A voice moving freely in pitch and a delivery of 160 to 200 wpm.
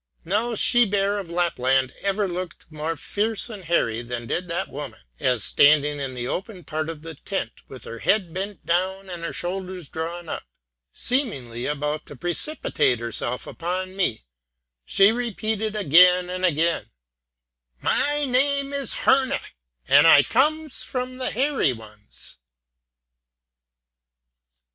No: wide, 6.3 semitones; average, 140 wpm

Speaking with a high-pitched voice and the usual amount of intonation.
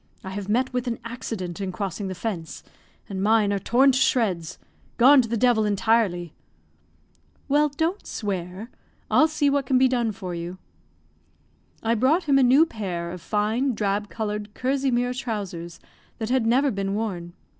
Yes: high, 220 Hz; average, 4.7 semitones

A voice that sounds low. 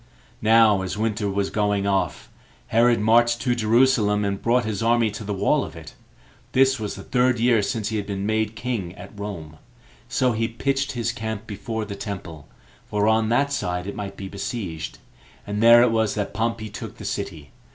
Yes: low, 110 Hz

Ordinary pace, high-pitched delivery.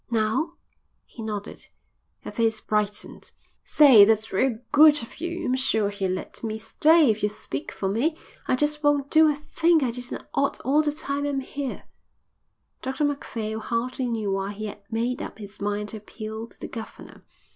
Yes: average, 180 wpm; high, 230 Hz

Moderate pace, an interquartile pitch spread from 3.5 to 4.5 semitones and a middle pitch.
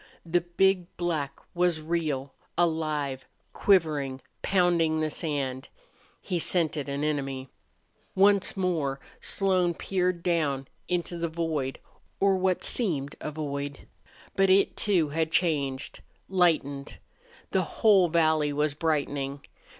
No: slow, 115 wpm; average, 3.8 semitones; medium, 160 Hz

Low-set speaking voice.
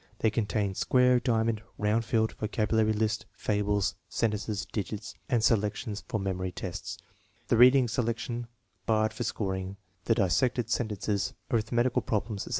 Yes: low, 110 Hz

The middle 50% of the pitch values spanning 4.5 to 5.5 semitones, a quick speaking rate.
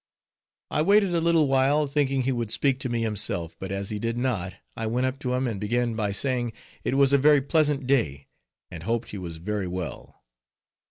Yes: average, 4.9 semitones; fast, 210 wpm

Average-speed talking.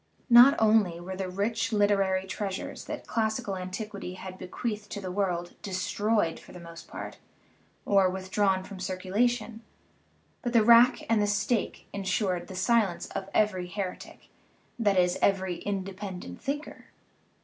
Yes: average, 145 wpm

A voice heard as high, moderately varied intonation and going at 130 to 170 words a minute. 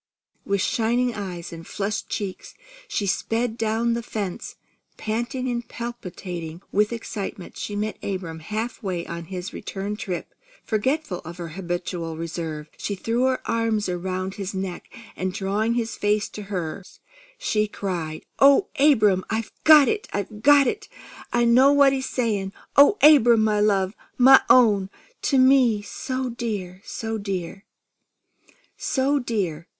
Yes: high, 210 Hz; average, 4.3 semitones; average, 145 wpm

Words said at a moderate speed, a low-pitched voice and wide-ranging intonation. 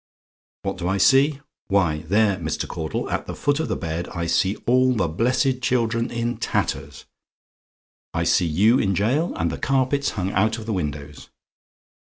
Yes: average, 180 wpm; low, 105 Hz; wide, 6.9 semitones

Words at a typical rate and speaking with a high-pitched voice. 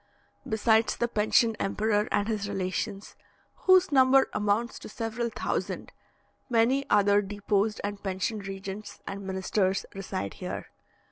No: slow, 125 wpm; high, 210 Hz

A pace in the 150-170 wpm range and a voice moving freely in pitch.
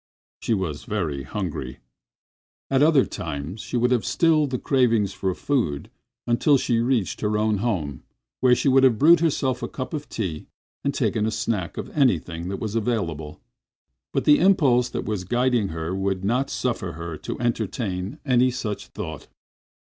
Yes: average, 160 wpm; wide, 5.7 semitones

